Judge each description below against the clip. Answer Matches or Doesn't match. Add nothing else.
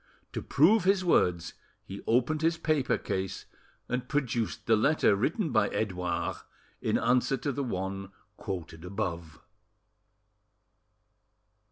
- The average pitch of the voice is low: Matches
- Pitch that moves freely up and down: Matches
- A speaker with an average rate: Doesn't match